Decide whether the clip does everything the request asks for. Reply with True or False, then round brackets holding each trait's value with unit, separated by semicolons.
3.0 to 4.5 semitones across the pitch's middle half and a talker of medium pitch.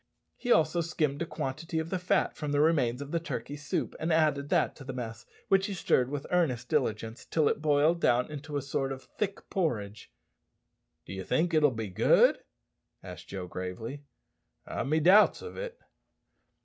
False (5.0 semitones; 145 Hz)